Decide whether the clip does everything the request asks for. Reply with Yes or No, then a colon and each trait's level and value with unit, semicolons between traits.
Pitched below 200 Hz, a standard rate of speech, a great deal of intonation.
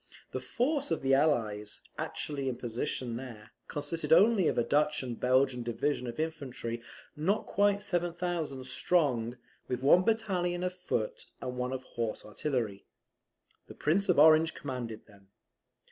Yes: medium, 140 Hz; average, 145 wpm; wide, 6.3 semitones